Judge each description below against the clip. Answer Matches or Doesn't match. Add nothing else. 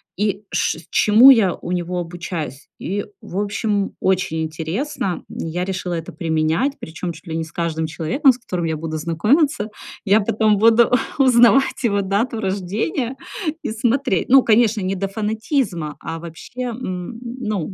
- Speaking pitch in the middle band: Doesn't match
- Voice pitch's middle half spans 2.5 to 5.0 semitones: Doesn't match